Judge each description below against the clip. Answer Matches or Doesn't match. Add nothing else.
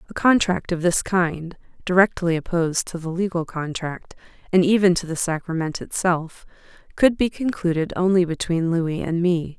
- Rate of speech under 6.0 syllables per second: Matches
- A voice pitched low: Doesn't match